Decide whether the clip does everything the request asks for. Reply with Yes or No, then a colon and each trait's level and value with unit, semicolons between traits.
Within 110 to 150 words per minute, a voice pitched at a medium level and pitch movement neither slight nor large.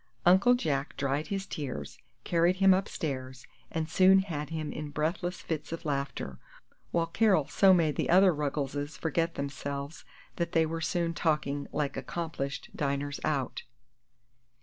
Yes: average, 145 wpm; medium, 155 Hz; average, 3.5 semitones